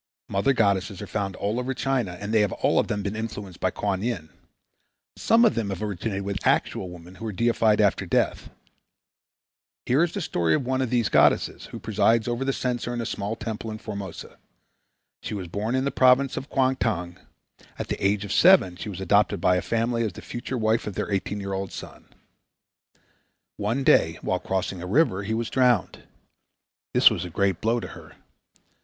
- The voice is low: Yes, low, 105 Hz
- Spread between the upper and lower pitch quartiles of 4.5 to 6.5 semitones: No, average, 3.8 semitones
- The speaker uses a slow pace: No, average, 200 wpm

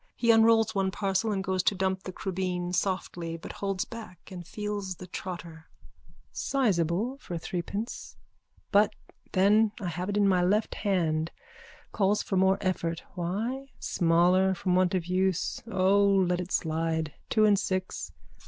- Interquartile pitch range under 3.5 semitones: Yes, narrow, 2.4 semitones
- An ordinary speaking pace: Yes, average, 155 wpm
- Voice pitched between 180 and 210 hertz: Yes, high, 190 Hz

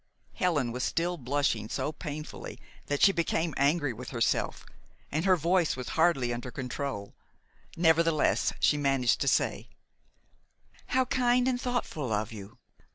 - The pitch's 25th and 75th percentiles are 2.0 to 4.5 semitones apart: No, wide, 5.4 semitones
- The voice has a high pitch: No, medium, 145 Hz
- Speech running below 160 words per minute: Yes, average, 140 wpm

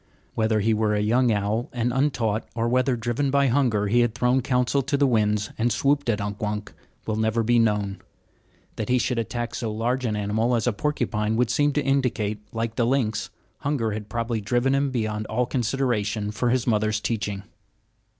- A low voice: Yes, low, 115 Hz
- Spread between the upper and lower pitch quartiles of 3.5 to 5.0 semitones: No, average, 2.8 semitones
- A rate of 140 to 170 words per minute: No, average, 200 wpm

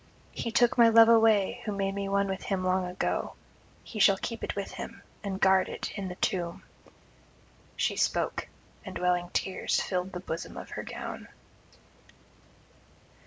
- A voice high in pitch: Yes, high, 195 Hz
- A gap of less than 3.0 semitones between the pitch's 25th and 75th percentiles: Yes, narrow, 2.4 semitones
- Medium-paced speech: Yes, average, 165 wpm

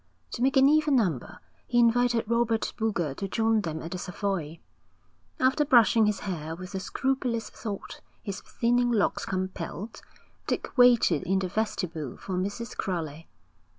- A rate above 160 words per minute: No, average, 150 wpm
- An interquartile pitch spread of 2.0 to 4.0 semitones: No, average, 4.7 semitones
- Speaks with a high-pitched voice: Yes, high, 210 Hz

